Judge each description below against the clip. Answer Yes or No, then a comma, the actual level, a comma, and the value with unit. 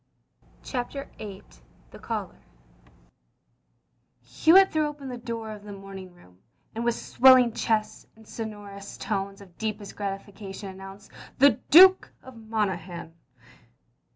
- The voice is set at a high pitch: Yes, high, 210 Hz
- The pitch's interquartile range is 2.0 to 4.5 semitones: Yes, average, 3.6 semitones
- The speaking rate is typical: No, slow, 120 wpm